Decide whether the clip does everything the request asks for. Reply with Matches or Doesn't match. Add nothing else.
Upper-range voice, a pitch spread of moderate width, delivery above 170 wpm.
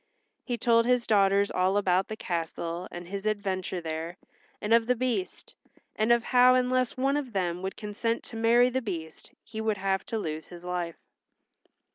Matches